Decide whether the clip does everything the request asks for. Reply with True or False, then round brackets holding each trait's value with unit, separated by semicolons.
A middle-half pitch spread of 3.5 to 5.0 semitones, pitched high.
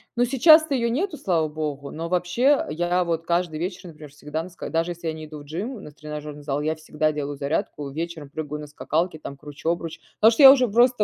False (3.8 semitones; 165 Hz)